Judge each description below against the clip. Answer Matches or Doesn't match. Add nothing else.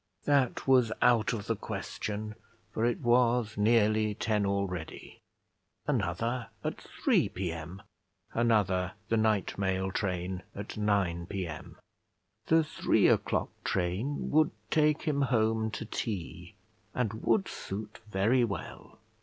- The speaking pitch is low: Matches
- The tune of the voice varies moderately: Matches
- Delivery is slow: Matches